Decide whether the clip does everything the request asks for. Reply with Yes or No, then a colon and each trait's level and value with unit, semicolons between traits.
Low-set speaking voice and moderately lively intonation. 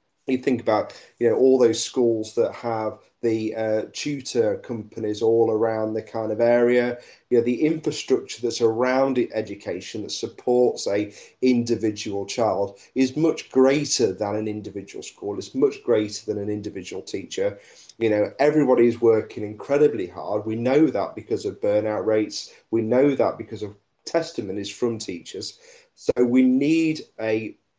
Yes: low, 115 Hz; average, 3.3 semitones